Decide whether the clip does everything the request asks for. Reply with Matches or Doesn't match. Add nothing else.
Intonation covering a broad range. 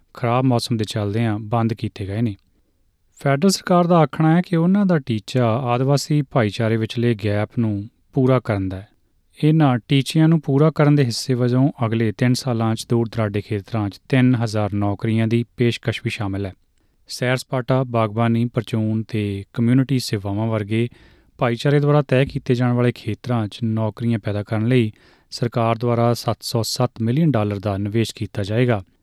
Doesn't match